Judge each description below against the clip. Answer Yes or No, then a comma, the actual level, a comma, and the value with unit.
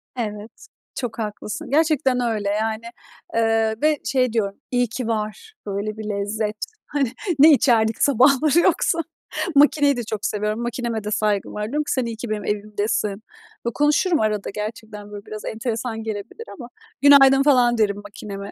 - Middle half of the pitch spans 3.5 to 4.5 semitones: Yes, average, 3.9 semitones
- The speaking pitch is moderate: No, high, 225 Hz